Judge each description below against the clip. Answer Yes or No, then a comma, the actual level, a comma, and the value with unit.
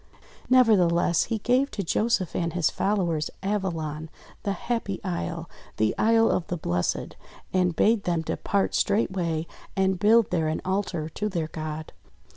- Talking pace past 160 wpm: No, average, 150 wpm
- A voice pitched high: No, medium, 180 Hz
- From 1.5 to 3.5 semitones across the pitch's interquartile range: No, average, 4.5 semitones